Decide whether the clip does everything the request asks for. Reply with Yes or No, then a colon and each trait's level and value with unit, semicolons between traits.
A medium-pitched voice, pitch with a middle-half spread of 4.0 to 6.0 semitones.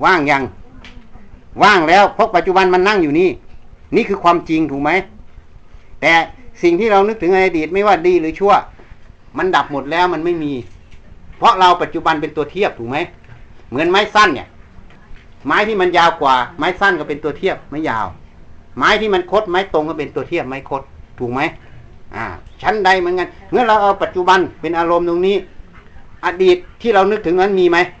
Yes: medium, 170 Hz; average, 5.2 semitones